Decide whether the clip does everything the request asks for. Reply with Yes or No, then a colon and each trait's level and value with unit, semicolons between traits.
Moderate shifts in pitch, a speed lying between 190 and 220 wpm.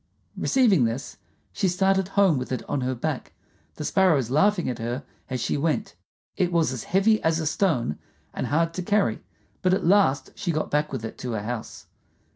No: wide, 6.9 semitones; average, 195 wpm